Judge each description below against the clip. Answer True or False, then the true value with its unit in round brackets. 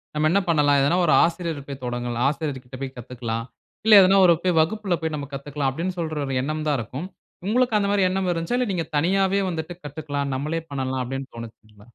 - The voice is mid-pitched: True (150 Hz)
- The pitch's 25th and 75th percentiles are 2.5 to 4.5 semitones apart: False (4.9 semitones)